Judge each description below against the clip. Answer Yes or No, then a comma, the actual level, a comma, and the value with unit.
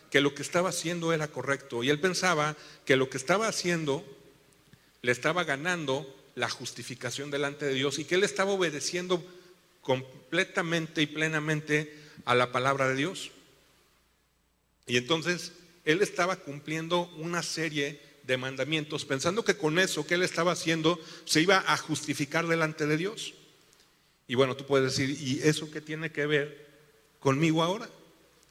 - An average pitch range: Yes, average, 3.9 semitones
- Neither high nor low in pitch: Yes, medium, 150 Hz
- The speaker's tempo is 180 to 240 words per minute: No, average, 155 wpm